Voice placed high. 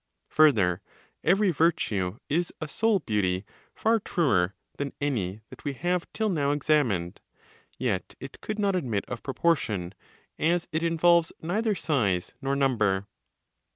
No: medium, 145 Hz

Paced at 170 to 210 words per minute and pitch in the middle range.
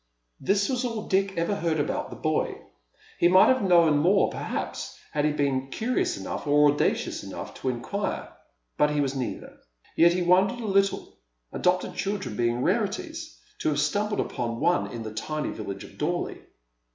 Yes: average, 175 wpm; medium, 175 Hz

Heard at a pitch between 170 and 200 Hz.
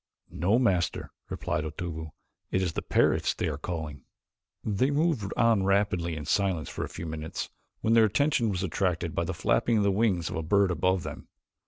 No: very low, 95 Hz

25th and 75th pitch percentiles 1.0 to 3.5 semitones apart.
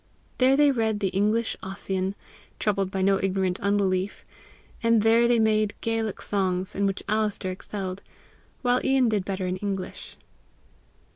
Yes: average, 2.7 semitones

